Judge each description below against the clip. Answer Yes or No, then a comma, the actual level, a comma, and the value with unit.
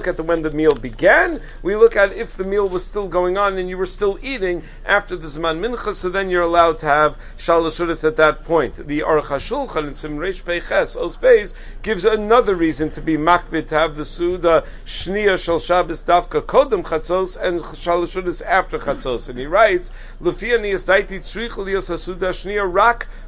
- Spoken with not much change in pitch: No, average, 3.7 semitones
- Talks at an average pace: Yes, average, 175 wpm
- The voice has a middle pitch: Yes, medium, 180 Hz